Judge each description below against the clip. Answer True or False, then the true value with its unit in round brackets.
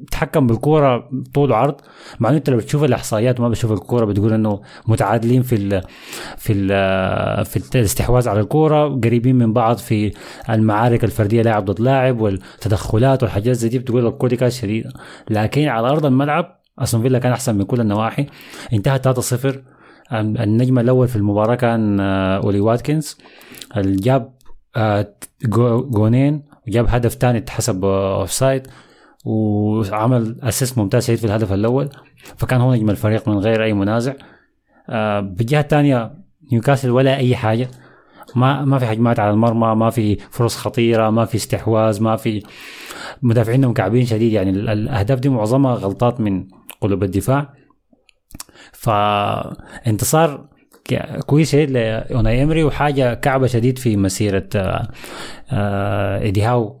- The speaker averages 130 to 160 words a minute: True (135 wpm)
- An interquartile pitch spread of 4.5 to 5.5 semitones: False (3.5 semitones)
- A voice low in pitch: True (115 Hz)